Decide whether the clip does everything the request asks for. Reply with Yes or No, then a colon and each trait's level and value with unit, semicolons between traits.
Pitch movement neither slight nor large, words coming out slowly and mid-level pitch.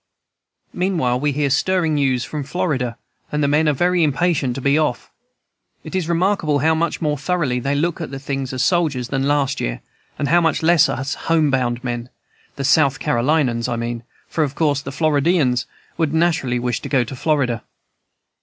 No: average, 4.0 semitones; average, 185 wpm; medium, 145 Hz